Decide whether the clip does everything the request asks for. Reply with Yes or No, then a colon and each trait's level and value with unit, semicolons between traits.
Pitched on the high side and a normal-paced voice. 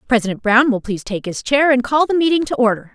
No: high, 245 Hz; fast, 265 wpm